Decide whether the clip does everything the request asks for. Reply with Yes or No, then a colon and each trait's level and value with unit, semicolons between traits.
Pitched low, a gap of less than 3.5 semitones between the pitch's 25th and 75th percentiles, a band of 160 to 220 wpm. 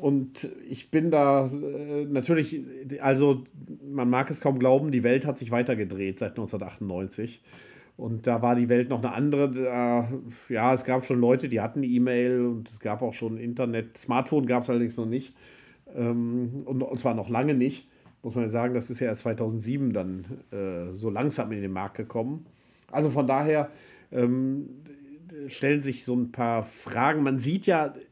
Yes: low, 125 Hz; average, 2.7 semitones; average, 180 wpm